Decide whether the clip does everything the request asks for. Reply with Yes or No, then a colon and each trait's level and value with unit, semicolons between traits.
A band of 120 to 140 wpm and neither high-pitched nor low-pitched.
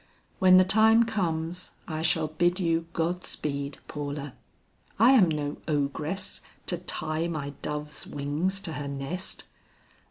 Yes: slow, 135 wpm; medium, 165 Hz